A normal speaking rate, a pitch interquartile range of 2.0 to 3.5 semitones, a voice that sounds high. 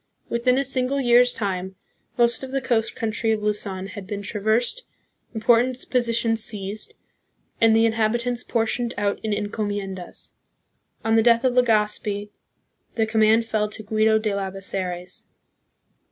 Yes: average, 155 wpm; narrow, 2.5 semitones; high, 220 Hz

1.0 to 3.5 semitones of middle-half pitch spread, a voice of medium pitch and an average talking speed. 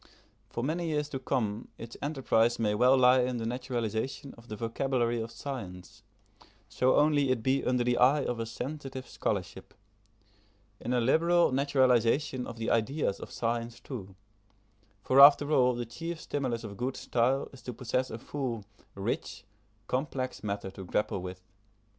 No: average, 2.9 semitones; low, 125 Hz; average, 160 wpm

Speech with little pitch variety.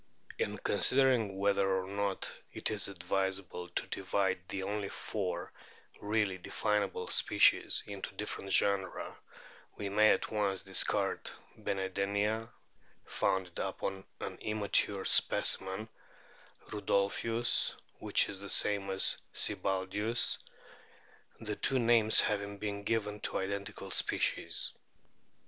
Yes: narrow, 1.6 semitones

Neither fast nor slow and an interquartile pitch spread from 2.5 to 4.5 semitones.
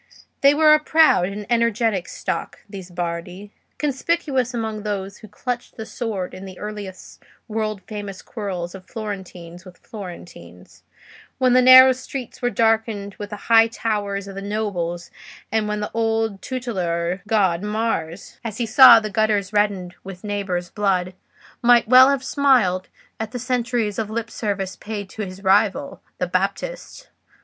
Yes: average, 155 wpm; average, 3.5 semitones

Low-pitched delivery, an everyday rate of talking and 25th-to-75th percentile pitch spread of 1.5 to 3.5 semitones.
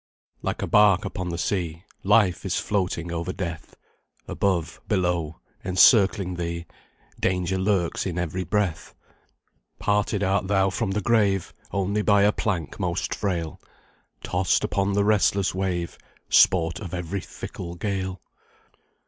No: very low, 95 Hz; slow, 130 wpm; narrow, 2.6 semitones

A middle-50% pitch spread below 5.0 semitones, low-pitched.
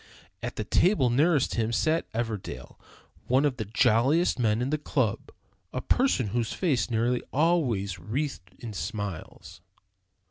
No: average, 5.3 semitones; low, 120 Hz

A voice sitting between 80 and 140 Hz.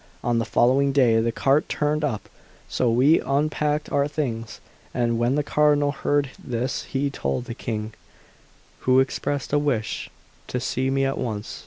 Yes: low, 135 Hz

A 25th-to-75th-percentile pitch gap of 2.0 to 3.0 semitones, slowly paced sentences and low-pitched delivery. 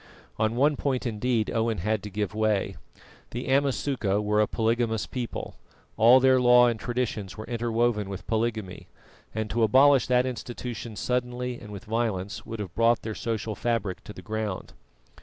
No: narrow, 2.5 semitones; average, 165 wpm; low, 115 Hz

